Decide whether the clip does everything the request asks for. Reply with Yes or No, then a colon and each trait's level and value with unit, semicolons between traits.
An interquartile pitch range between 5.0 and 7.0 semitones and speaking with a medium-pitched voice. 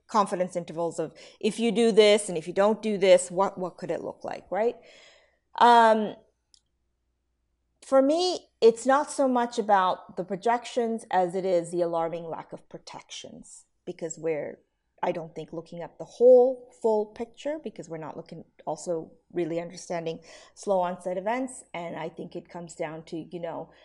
Yes: average, 5.3 semitones; medium, 180 Hz